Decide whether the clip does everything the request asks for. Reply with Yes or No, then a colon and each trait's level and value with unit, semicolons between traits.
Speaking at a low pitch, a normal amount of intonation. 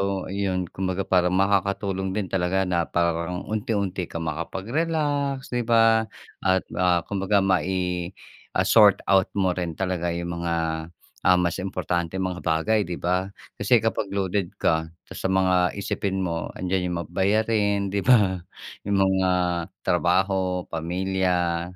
No: very low, 95 Hz; narrow, 1.9 semitones